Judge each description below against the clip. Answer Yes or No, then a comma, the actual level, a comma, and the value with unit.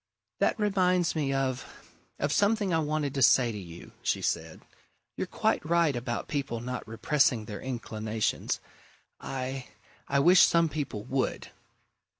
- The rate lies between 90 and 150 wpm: Yes, average, 145 wpm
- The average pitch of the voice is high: No, low, 135 Hz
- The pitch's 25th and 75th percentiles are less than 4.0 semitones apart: No, average, 5.3 semitones